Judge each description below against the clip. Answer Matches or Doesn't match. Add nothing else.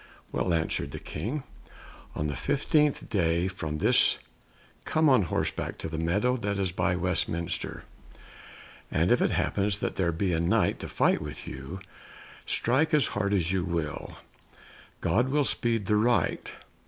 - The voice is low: Matches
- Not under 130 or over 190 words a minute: Matches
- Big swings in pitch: Matches